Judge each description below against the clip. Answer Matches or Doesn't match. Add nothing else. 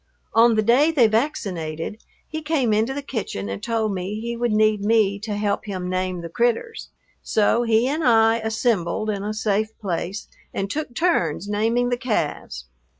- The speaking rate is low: Doesn't match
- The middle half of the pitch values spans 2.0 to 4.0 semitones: Matches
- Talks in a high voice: Matches